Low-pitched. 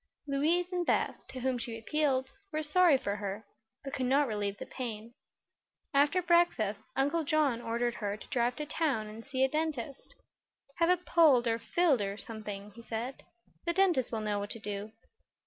No: very high, 255 Hz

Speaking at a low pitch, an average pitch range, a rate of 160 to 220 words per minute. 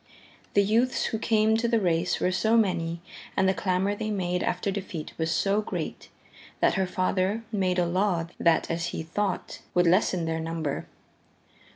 No: medium, 185 Hz; average, 3.3 semitones; average, 175 wpm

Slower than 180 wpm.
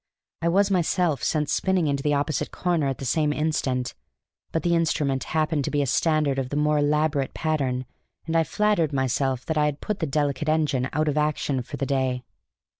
No: average, 200 wpm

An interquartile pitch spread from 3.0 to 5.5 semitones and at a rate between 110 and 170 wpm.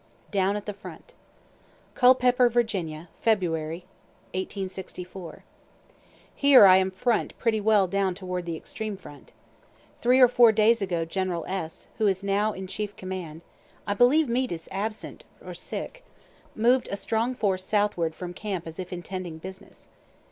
Yes: average, 3.4 semitones; average, 145 wpm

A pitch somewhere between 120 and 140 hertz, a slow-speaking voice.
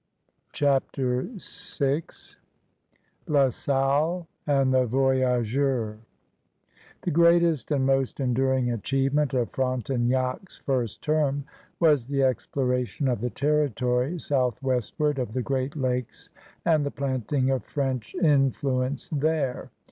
Yes: low, 135 Hz; slow, 105 wpm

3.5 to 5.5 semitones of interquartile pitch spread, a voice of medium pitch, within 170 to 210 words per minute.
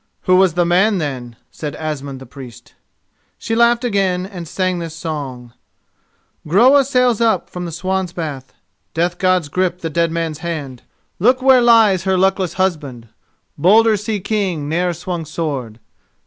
No: average, 4.3 semitones; medium, 175 Hz; average, 155 wpm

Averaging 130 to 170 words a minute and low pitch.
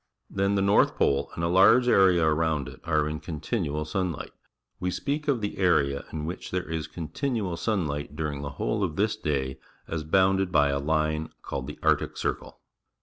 No: average, 195 wpm; very low, 80 Hz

